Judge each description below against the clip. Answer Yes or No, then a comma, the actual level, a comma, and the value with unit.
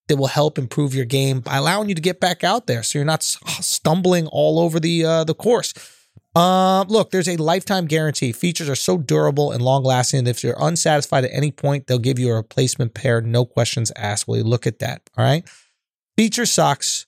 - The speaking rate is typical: No, fast, 220 wpm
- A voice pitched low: No, medium, 145 Hz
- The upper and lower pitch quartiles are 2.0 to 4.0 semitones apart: No, average, 4.9 semitones